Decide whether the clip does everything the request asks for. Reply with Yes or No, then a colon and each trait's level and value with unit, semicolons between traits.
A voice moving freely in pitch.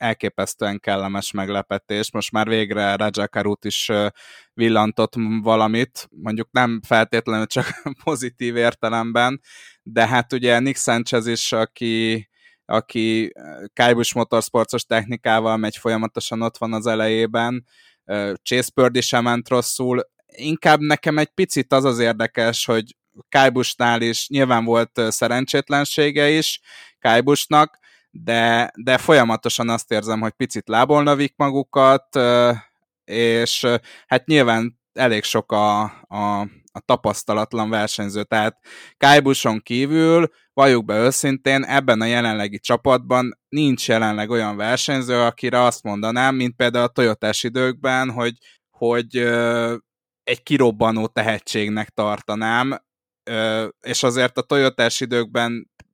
No: narrow, 2.5 semitones